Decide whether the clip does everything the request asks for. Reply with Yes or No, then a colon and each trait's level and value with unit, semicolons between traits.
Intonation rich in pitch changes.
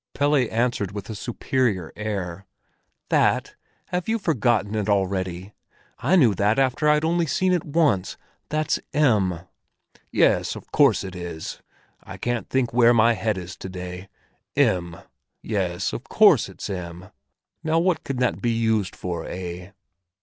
Yes: wide, 6.5 semitones